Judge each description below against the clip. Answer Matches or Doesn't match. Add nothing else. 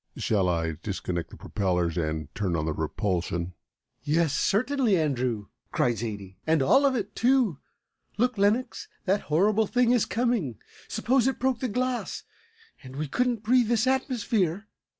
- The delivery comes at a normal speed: Matches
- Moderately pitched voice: Matches